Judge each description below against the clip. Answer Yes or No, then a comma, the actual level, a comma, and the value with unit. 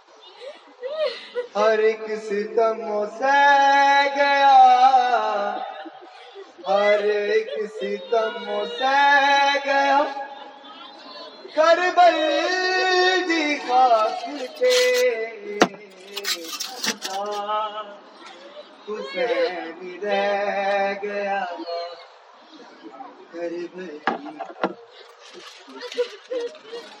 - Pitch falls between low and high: No, very high, 275 Hz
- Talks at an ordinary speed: No, slow, 40 wpm